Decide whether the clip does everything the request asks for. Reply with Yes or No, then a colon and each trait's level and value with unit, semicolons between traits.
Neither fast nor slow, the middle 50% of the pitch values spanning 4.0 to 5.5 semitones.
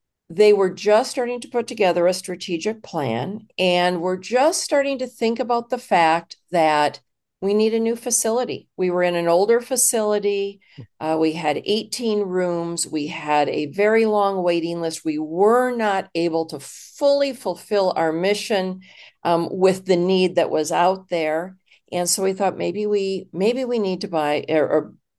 Yes: average, 170 wpm; average, 4.3 semitones